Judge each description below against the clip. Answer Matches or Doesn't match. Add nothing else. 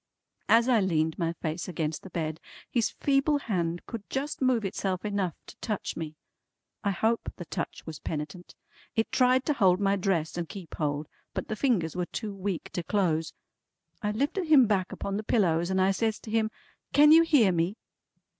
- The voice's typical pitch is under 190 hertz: Doesn't match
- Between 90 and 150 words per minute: Doesn't match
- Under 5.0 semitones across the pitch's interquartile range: Doesn't match